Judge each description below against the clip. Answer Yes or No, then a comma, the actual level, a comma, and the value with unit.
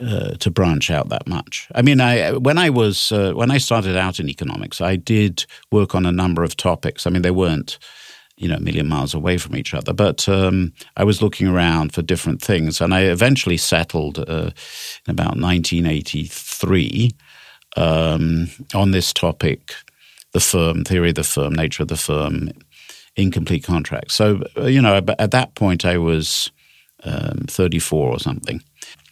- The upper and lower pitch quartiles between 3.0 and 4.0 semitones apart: No, average, 5.2 semitones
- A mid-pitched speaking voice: No, very low, 95 Hz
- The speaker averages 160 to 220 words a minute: Yes, average, 175 wpm